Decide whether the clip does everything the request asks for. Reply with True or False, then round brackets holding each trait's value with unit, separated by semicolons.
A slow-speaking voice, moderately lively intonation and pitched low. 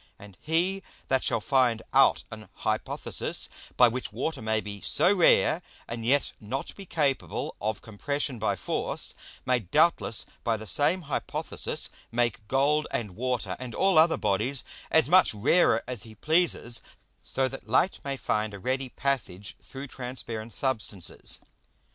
False (150 wpm; 4.6 semitones; 130 Hz)